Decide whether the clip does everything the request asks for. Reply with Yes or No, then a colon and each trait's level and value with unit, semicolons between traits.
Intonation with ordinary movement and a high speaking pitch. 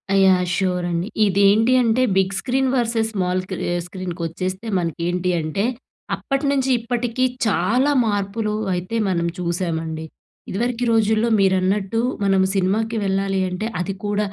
Yes: average, 3.7 semitones; high, 195 Hz